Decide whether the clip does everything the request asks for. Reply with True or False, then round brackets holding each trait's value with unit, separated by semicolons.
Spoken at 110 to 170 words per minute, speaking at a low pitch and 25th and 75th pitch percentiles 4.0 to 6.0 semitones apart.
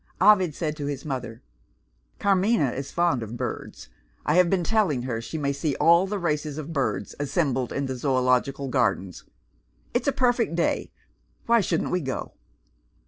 False (165 wpm; 145 Hz; 5.6 semitones)